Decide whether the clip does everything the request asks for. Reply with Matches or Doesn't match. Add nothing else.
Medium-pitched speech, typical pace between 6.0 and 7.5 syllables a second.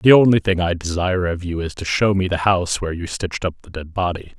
Doesn't match